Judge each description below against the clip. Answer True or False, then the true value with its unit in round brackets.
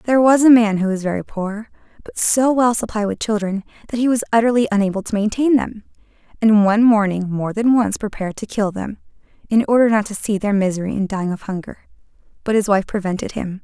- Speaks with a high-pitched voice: True (210 Hz)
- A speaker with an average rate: False (210 wpm)